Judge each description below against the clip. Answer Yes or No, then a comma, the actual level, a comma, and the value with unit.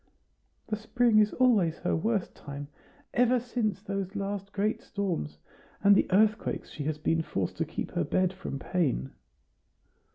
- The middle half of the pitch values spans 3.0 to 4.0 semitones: No, average, 4.9 semitones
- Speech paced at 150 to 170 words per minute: Yes, average, 155 wpm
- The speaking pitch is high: Yes, high, 195 Hz